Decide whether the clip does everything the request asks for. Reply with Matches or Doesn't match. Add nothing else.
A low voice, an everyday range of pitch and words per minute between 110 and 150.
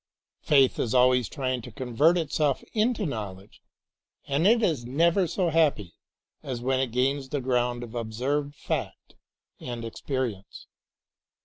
Matches